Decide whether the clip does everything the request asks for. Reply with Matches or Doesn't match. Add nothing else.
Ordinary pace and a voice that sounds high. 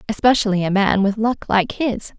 Matches